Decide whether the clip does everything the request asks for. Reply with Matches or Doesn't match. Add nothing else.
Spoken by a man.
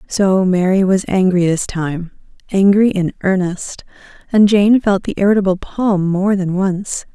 Doesn't match